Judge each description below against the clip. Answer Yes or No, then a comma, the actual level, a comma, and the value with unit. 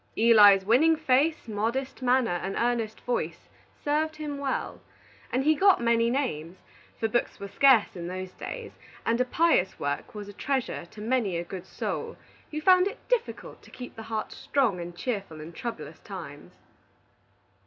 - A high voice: Yes, high, 235 Hz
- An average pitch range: No, wide, 5.8 semitones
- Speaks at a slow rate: No, average, 165 wpm